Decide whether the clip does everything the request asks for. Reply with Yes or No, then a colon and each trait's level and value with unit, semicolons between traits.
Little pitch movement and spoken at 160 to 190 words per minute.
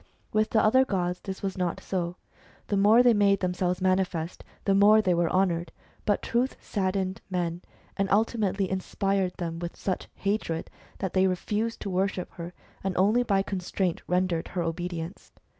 Yes: narrow, 2.2 semitones; average, 165 wpm